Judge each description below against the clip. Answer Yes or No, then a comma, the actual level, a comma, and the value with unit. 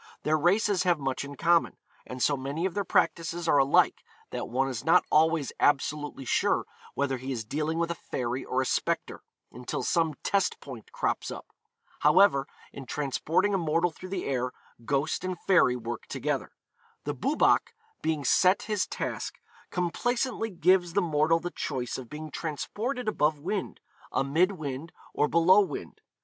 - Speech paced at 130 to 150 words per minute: No, average, 165 wpm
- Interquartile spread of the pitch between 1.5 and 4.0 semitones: No, average, 4.8 semitones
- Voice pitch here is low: No, medium, 155 Hz